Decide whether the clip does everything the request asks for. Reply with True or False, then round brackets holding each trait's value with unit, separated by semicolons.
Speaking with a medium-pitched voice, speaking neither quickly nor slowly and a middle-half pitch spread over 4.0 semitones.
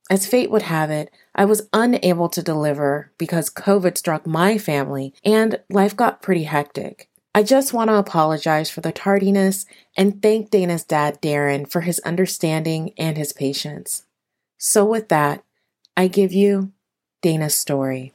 True (175 Hz; 155 wpm; 4.7 semitones)